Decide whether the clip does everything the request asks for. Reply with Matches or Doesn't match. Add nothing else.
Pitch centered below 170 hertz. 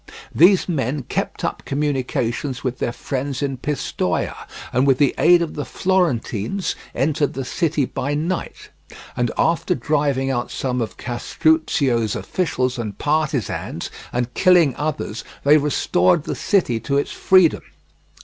Matches